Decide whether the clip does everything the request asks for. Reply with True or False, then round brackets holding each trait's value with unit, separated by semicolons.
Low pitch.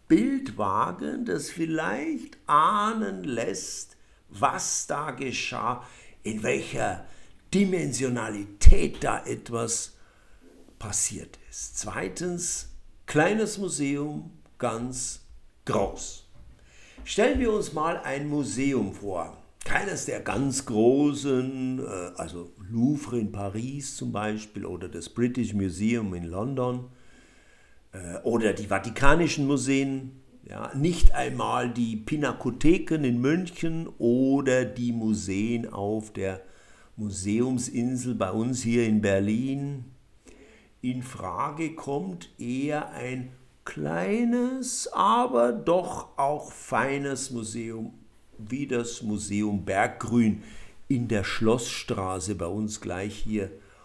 True (125 Hz)